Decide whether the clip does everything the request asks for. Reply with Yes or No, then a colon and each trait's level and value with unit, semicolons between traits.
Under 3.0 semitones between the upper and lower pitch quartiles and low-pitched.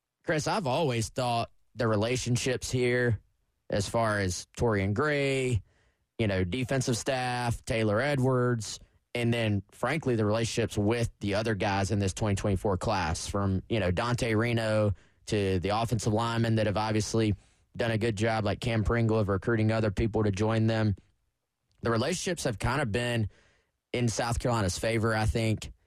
Yes: narrow, 2.6 semitones; low, 110 Hz